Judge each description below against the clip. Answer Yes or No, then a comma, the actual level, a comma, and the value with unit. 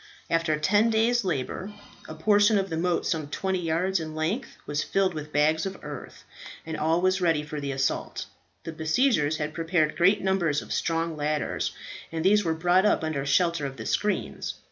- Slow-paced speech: No, average, 190 wpm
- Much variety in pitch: No, average, 3.8 semitones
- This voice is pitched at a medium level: Yes, medium, 165 Hz